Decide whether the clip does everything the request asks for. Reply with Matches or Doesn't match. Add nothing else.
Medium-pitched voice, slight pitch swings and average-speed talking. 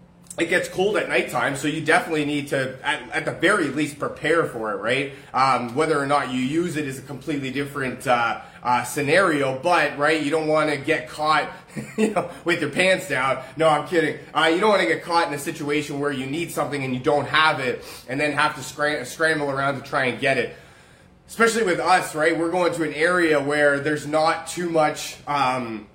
Doesn't match